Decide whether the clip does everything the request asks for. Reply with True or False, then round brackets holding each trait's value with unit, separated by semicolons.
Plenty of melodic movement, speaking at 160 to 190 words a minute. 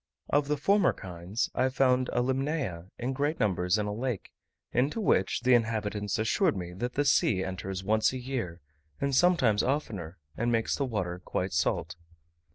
True (6.1 semitones; 170 wpm)